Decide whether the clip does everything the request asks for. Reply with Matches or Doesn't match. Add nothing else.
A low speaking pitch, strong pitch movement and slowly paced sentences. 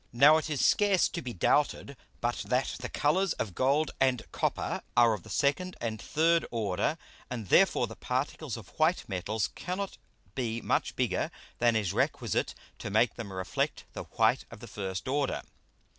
Doesn't match